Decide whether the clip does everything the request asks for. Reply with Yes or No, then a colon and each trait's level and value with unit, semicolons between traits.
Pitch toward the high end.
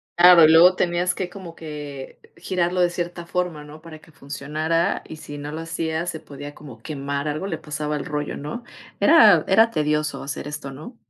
No: medium, 155 Hz